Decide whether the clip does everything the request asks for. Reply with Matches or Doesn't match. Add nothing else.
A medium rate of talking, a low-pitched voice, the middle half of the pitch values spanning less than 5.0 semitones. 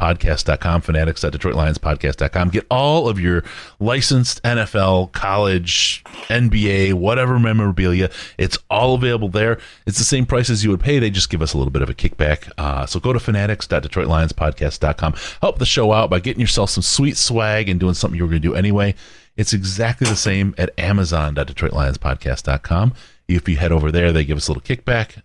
Doesn't match